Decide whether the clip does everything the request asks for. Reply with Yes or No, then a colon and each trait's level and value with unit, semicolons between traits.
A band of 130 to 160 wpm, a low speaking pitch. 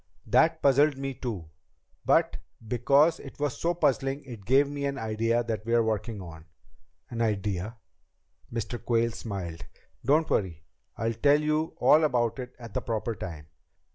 Yes: average, 155 wpm; low, 115 Hz